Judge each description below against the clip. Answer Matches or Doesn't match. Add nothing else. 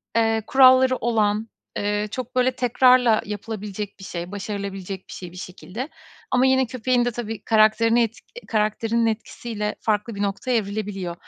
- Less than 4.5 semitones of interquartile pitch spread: Matches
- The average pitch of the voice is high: Matches